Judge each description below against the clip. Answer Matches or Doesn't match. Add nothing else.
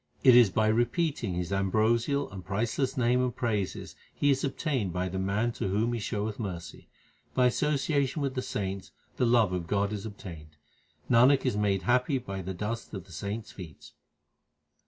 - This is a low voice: Matches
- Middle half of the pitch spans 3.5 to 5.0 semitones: Matches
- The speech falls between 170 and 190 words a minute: Matches